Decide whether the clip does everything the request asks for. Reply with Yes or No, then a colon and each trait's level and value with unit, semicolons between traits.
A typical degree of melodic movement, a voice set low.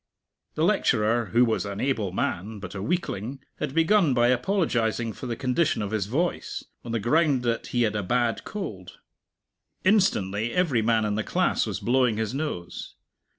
Yes: average, 4.6 semitones; low, 120 Hz